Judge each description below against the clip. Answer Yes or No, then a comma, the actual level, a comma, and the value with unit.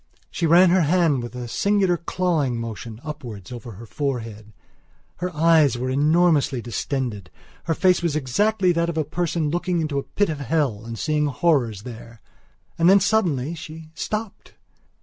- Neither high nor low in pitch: Yes, medium, 150 Hz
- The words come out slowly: No, average, 165 wpm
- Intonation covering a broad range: Yes, wide, 6.0 semitones